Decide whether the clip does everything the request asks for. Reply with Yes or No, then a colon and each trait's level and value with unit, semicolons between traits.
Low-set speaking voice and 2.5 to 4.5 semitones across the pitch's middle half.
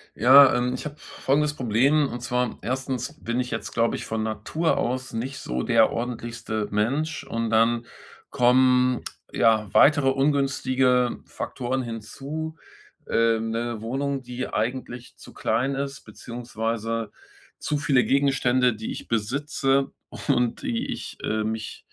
Yes: low, 125 Hz; average, 2.9 semitones